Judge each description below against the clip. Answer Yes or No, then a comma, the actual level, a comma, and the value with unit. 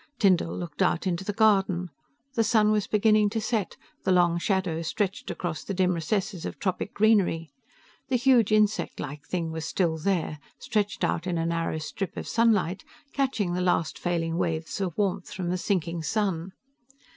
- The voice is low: No, medium, 185 Hz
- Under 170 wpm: No, average, 175 wpm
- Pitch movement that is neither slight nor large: Yes, average, 3.9 semitones